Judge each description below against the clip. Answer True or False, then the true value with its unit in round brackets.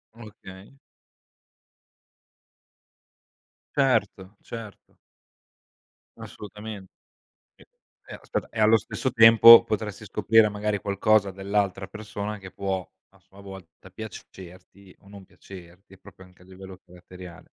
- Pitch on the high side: False (100 Hz)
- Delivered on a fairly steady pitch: True (2.2 semitones)